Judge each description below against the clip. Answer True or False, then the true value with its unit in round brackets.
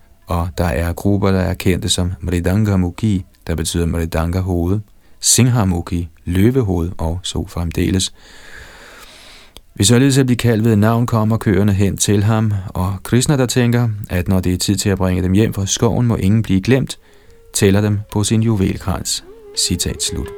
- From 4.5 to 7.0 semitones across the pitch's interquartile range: False (3.8 semitones)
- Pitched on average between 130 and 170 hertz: False (100 Hz)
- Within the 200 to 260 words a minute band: False (170 wpm)